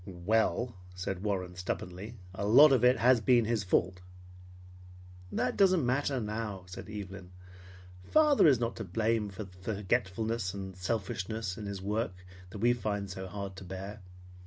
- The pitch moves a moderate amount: Yes, average, 3.6 semitones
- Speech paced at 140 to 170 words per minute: Yes, average, 160 wpm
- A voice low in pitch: Yes, low, 105 Hz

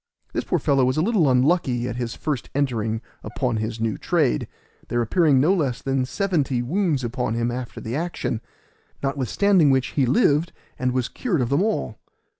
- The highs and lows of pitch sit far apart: No, average, 4.3 semitones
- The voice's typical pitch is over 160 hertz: No, low, 130 Hz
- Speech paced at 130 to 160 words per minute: No, average, 180 wpm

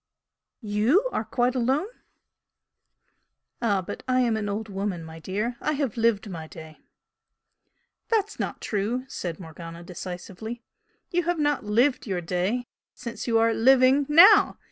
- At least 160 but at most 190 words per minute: No, average, 145 wpm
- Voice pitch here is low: No, high, 225 Hz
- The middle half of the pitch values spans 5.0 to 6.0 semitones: Yes, wide, 5.5 semitones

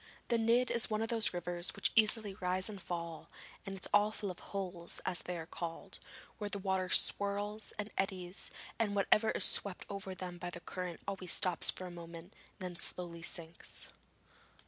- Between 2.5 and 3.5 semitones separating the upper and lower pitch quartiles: Yes, average, 2.8 semitones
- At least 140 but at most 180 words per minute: No, average, 190 wpm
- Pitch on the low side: No, medium, 185 Hz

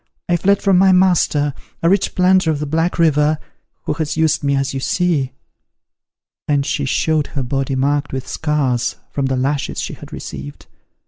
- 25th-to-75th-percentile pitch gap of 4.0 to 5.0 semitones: No, average, 3.5 semitones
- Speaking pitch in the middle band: Yes, medium, 150 Hz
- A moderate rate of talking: Yes, average, 180 wpm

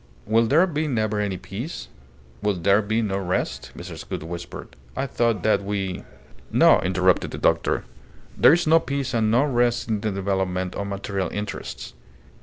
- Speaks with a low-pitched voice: Yes, low, 105 Hz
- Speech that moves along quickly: No, average, 175 wpm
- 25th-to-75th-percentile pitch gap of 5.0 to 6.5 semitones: No, average, 3.8 semitones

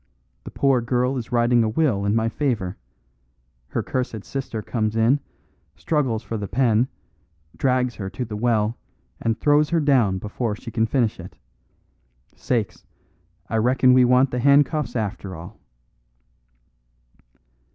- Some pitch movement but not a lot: Yes, average, 3.1 semitones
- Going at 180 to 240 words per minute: No, average, 140 wpm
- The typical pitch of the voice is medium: No, low, 120 Hz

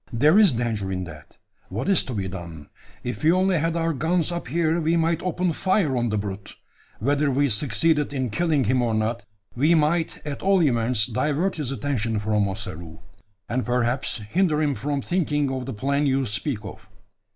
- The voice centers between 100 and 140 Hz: Yes, low, 135 Hz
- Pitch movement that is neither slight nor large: No, wide, 6.4 semitones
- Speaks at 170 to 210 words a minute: Yes, average, 190 wpm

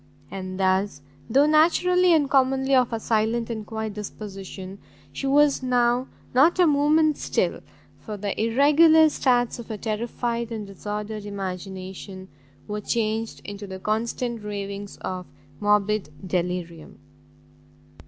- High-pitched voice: Yes, high, 220 Hz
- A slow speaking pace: Yes, slow, 125 wpm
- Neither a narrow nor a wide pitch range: Yes, average, 4.7 semitones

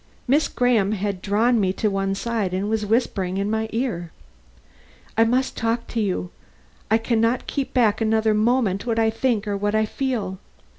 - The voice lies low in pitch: No, high, 220 Hz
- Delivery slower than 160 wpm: No, average, 185 wpm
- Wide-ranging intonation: No, average, 2.7 semitones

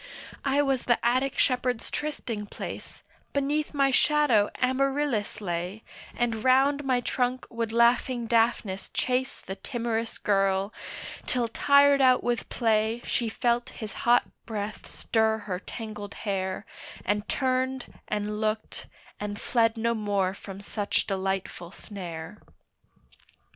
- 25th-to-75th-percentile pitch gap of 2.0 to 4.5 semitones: Yes, average, 3.7 semitones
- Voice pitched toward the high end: Yes, high, 230 Hz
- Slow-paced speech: Yes, slow, 125 wpm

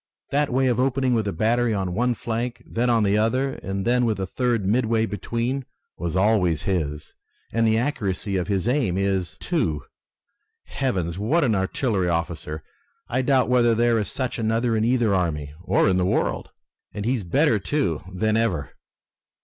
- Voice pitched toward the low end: Yes, low, 110 Hz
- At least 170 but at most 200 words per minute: Yes, average, 180 wpm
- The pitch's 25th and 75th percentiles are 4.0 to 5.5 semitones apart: Yes, average, 4.7 semitones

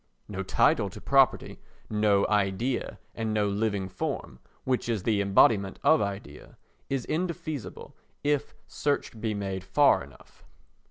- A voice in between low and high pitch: No, low, 105 Hz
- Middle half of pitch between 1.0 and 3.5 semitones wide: No, average, 4.8 semitones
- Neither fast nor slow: No, slow, 130 wpm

